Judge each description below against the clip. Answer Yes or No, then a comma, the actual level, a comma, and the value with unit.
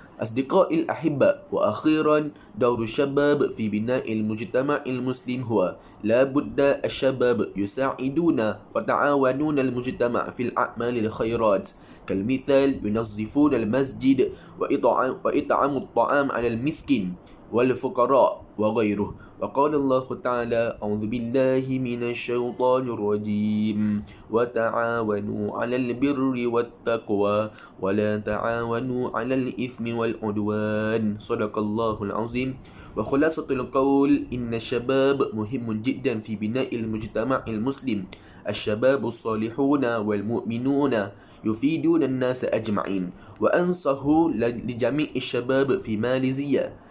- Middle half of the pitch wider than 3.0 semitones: Yes, average, 3.7 semitones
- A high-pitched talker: No, low, 120 Hz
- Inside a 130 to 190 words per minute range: No, slow, 90 wpm